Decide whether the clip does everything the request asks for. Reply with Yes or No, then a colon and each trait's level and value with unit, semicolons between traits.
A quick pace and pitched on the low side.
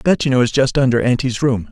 Yes: fast, 280 wpm; low, 125 Hz